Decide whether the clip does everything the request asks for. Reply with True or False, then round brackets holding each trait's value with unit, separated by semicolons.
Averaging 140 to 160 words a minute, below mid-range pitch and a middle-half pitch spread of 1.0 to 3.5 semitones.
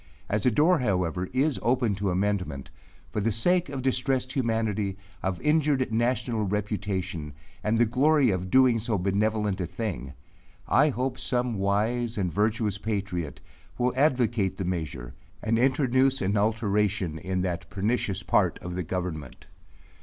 False (145 wpm; 105 Hz; 4.8 semitones)